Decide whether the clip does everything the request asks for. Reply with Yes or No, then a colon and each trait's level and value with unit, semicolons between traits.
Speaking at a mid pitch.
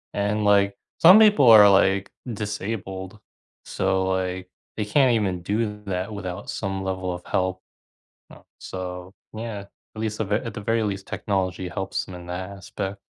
No: low, 100 Hz